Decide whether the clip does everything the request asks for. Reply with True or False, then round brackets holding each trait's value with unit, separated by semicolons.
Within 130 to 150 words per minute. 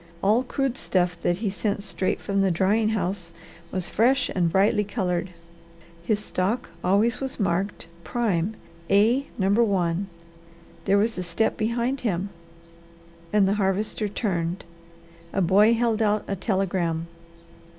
True (140 wpm)